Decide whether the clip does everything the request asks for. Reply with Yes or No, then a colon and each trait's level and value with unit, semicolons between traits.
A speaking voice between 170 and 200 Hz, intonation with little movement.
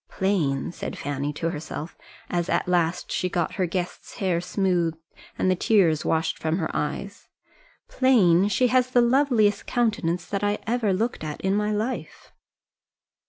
No: medium, 185 Hz; average, 4.1 semitones